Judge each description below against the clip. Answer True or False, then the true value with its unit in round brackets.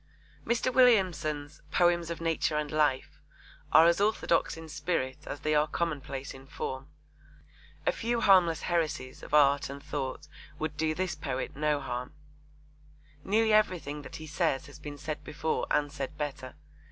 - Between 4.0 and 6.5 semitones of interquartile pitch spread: False (3.1 semitones)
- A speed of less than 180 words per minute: True (155 wpm)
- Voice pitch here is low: False (150 Hz)